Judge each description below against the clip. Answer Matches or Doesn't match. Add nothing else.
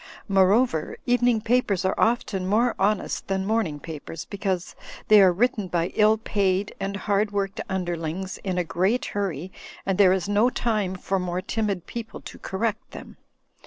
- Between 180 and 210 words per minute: Doesn't match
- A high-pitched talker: Matches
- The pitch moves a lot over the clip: Doesn't match